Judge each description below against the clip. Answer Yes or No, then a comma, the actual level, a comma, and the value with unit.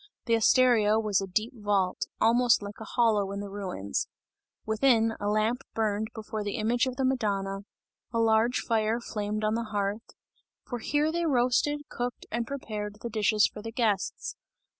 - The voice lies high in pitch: Yes, high, 220 Hz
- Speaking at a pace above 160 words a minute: Yes, average, 170 wpm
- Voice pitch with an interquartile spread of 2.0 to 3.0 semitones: Yes, narrow, 2.6 semitones